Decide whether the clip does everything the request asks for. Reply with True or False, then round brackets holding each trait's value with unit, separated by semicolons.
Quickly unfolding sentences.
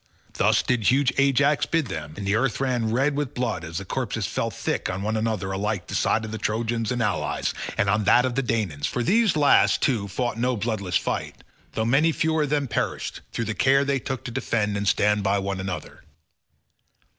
True (215 wpm)